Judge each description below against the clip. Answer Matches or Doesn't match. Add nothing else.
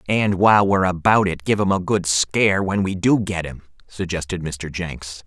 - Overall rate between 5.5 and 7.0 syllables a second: Doesn't match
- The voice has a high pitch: Doesn't match